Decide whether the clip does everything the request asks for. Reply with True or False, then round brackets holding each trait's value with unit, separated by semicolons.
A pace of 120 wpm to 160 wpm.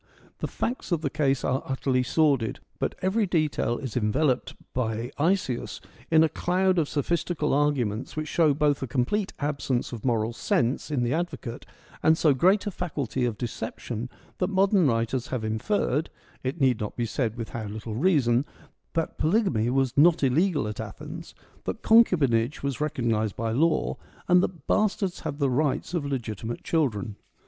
False (170 wpm)